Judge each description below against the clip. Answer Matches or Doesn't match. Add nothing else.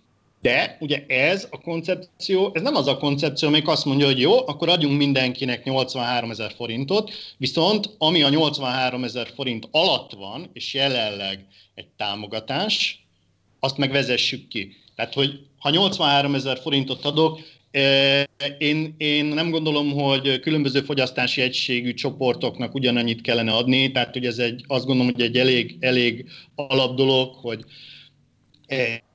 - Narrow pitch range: Doesn't match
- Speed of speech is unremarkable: Matches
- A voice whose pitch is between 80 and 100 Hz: Doesn't match